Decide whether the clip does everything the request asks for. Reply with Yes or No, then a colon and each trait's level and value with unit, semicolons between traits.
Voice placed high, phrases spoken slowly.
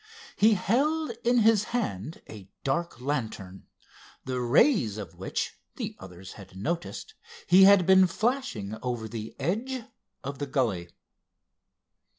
No: medium, 140 Hz; slow, 130 wpm